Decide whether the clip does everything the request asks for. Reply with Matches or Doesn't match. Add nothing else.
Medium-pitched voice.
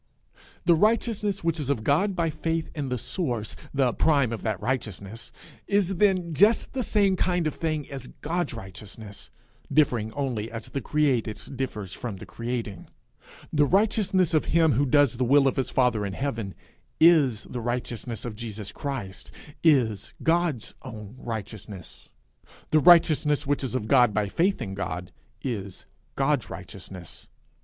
Doesn't match